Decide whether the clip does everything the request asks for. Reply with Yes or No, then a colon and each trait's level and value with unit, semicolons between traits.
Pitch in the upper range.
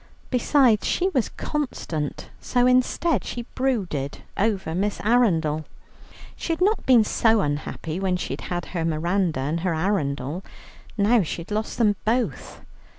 Yes: high, 200 Hz